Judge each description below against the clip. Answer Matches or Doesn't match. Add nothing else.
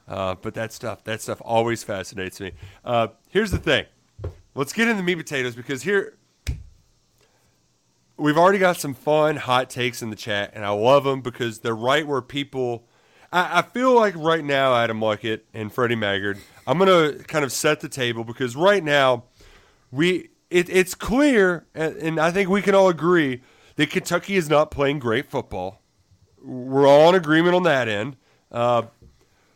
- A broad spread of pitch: Matches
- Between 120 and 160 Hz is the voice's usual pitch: Matches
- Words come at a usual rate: Matches